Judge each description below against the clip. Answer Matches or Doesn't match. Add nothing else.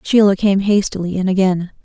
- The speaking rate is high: Doesn't match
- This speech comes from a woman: Matches